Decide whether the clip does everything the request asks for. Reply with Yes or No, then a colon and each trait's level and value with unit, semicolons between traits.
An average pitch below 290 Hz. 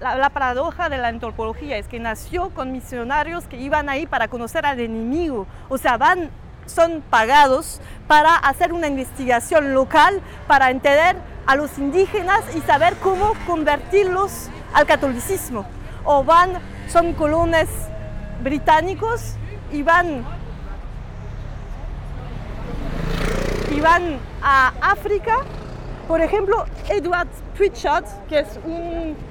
No: very high, 310 Hz